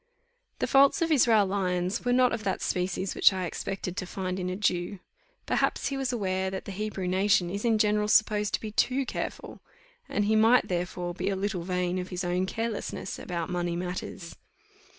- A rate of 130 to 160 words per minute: No, average, 195 wpm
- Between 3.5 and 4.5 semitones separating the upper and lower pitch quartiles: No, average, 3.0 semitones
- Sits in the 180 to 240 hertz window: Yes, high, 190 Hz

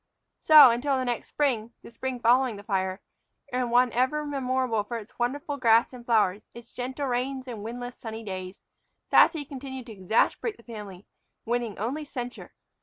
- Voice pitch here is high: Yes, high, 245 Hz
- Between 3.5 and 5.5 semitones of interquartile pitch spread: No, average, 2.8 semitones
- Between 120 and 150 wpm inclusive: No, average, 170 wpm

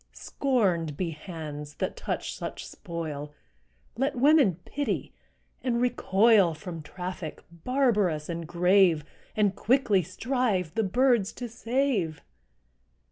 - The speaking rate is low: Yes, slow, 110 wpm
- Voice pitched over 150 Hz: Yes, high, 190 Hz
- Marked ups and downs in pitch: Yes, wide, 6.8 semitones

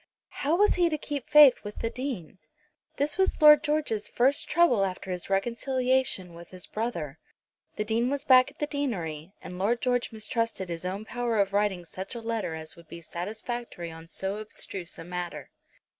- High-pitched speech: Yes, high, 220 Hz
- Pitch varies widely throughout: Yes, wide, 6.3 semitones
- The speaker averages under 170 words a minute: No, average, 185 wpm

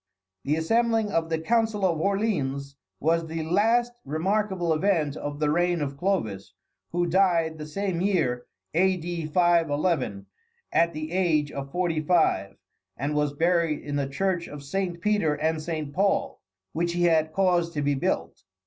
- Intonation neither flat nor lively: Yes, average, 3.7 semitones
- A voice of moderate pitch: Yes, medium, 165 Hz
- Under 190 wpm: Yes, average, 160 wpm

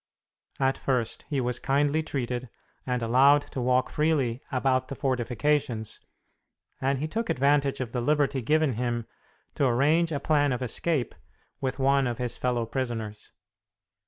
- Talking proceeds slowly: No, average, 150 wpm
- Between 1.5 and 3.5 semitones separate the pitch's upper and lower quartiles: Yes, average, 2.7 semitones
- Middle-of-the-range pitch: No, low, 130 Hz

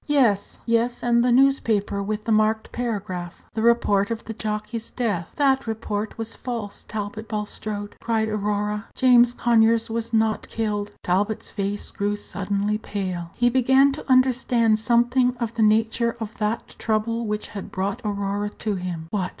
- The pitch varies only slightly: Yes, narrow, 2.3 semitones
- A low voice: No, high, 220 Hz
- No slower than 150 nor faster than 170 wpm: Yes, average, 160 wpm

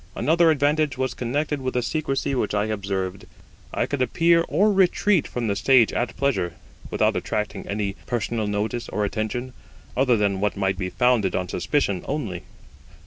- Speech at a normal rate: Yes, average, 165 wpm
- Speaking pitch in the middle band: No, low, 120 Hz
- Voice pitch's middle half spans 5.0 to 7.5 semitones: Yes, wide, 5.5 semitones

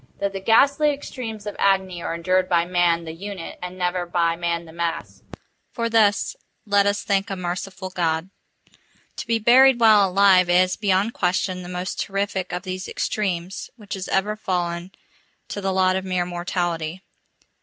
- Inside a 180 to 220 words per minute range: No, average, 165 wpm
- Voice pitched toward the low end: No, medium, 185 Hz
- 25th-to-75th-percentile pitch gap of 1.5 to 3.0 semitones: Yes, narrow, 2.4 semitones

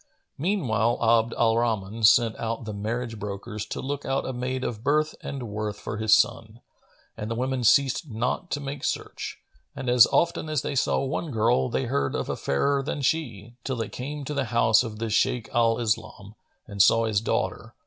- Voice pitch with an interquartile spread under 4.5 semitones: Yes, average, 3.6 semitones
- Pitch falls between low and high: No, low, 115 Hz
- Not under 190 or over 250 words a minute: Yes, average, 200 wpm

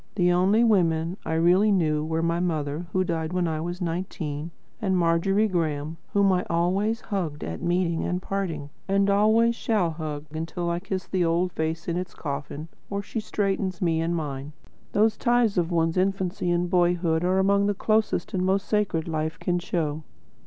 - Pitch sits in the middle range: Yes, medium, 175 Hz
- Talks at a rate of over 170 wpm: Yes, average, 180 wpm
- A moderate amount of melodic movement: Yes, average, 3.2 semitones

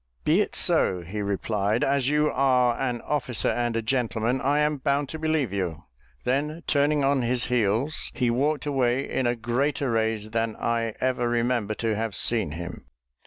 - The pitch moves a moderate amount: Yes, average, 3.7 semitones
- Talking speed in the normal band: Yes, average, 175 wpm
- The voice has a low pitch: Yes, low, 120 Hz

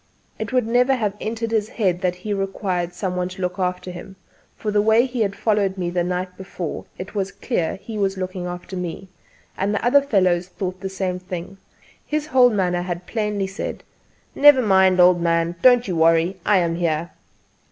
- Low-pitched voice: No, high, 190 Hz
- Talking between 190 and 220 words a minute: Yes, average, 195 wpm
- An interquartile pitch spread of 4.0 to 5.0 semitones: No, average, 3.0 semitones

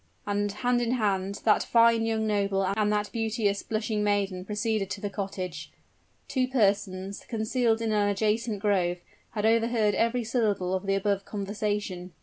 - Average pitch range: No, narrow, 2.2 semitones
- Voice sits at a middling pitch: No, high, 210 Hz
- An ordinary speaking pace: Yes, average, 155 wpm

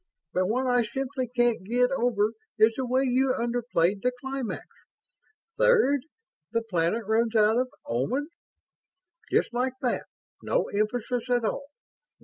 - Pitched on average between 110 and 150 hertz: No, high, 245 Hz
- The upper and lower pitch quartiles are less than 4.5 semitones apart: Yes, average, 2.9 semitones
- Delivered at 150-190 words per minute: No, slow, 135 wpm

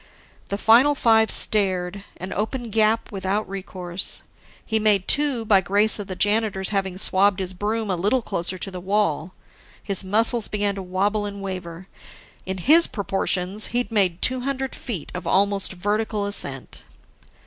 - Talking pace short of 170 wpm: Yes, average, 160 wpm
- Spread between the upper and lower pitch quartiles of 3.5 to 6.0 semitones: No, average, 2.7 semitones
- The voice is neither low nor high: No, high, 200 Hz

